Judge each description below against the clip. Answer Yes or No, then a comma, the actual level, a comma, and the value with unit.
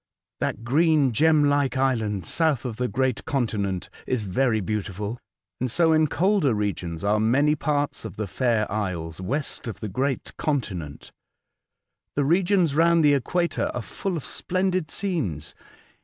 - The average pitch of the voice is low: Yes, low, 130 Hz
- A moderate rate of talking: Yes, average, 150 wpm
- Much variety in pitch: Yes, wide, 6.6 semitones